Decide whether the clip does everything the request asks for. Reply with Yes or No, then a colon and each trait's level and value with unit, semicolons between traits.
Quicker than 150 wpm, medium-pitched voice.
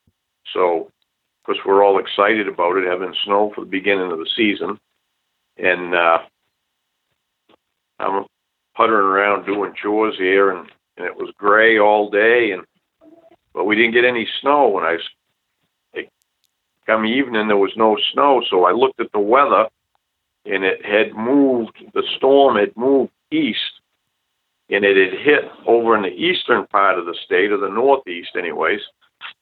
No: average, 160 wpm; low, 110 Hz